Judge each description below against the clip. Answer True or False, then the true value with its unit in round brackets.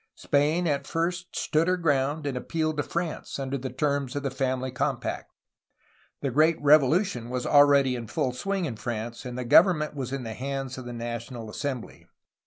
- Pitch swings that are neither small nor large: True (3.4 semitones)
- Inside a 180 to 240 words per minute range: True (185 wpm)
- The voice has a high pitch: False (140 Hz)